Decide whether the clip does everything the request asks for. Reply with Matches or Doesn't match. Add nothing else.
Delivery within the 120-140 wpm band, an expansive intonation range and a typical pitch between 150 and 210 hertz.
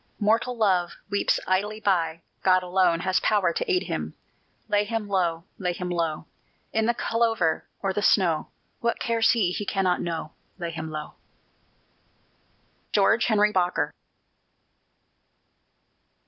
Doesn't match